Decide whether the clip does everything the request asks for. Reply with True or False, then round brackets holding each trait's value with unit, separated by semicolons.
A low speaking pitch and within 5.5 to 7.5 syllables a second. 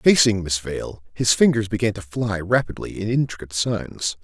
False (105 Hz; 4.9 syllables/s)